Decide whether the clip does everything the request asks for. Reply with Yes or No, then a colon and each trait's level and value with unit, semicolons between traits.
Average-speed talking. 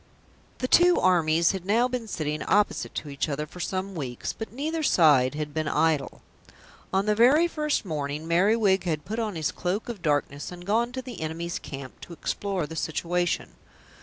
Yes: average, 185 wpm